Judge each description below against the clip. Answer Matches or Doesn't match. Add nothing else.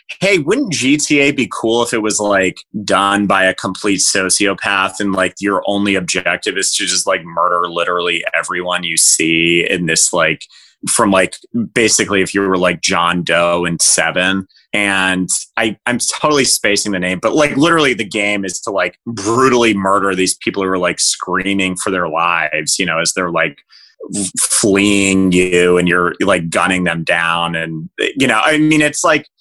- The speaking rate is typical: Matches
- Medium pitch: Doesn't match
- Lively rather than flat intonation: Doesn't match